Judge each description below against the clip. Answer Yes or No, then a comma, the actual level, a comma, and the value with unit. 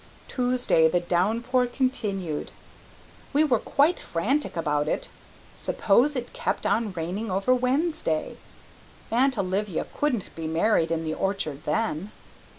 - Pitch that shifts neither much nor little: No, wide, 7.0 semitones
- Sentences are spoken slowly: Yes, slow, 125 wpm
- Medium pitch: No, high, 210 Hz